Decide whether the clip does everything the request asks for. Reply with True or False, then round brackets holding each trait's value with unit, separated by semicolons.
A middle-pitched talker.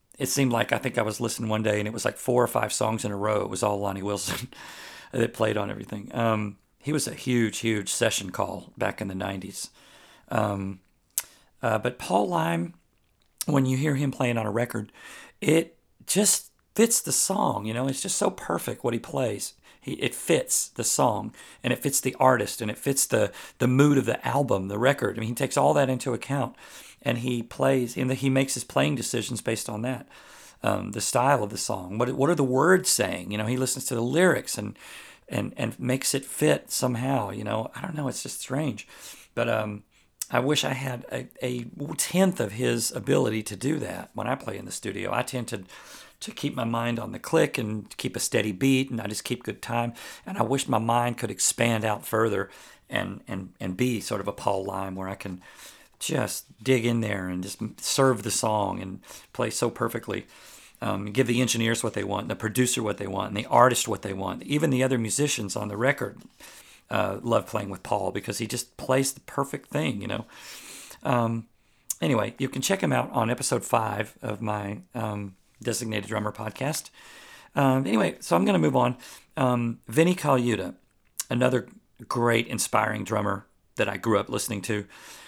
False (120 Hz)